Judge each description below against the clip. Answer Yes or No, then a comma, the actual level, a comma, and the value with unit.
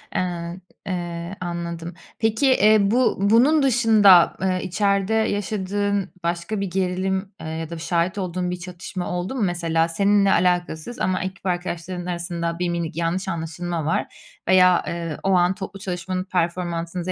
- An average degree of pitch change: No, narrow, 2.3 semitones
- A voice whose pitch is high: No, medium, 180 Hz